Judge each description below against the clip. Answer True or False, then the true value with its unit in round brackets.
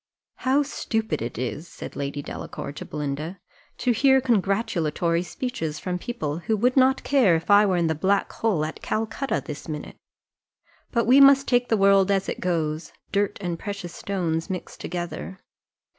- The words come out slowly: False (170 wpm)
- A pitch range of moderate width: False (5.8 semitones)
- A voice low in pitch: False (190 Hz)